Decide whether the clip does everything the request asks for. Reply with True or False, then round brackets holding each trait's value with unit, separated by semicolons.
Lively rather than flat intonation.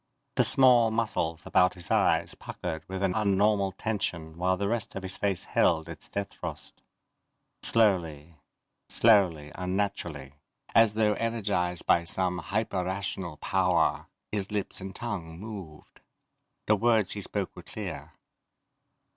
False (3.4 semitones)